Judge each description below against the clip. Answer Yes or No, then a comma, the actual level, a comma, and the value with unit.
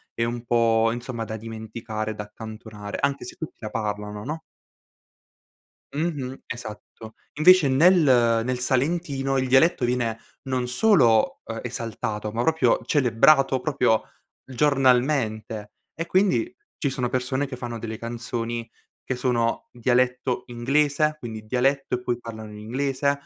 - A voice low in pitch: Yes, low, 125 Hz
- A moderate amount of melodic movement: Yes, average, 3.3 semitones